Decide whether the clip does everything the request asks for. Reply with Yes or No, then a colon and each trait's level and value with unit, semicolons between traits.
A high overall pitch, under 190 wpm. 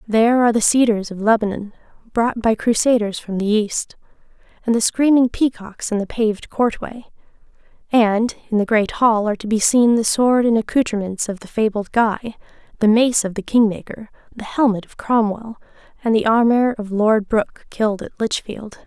Yes: high, 220 Hz; average, 175 wpm